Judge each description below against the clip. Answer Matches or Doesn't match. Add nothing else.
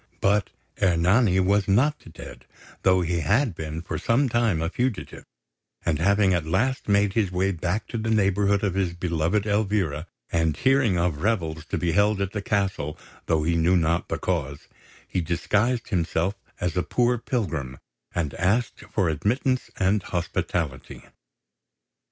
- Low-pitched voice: Matches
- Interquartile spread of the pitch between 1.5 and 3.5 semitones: Doesn't match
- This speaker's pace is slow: Doesn't match